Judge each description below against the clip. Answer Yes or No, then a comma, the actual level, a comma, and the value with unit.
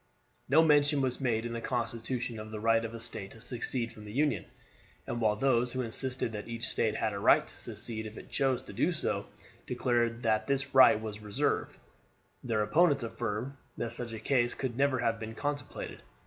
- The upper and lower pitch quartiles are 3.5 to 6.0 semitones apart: No, average, 2.9 semitones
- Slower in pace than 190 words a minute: No, fast, 205 wpm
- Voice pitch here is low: Yes, low, 115 Hz